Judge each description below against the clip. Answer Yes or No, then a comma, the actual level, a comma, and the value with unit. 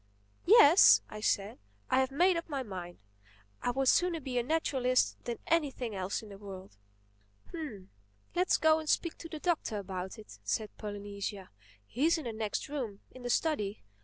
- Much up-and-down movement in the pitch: Yes, wide, 7.5 semitones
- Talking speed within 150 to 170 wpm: Yes, average, 165 wpm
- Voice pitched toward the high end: Yes, high, 245 Hz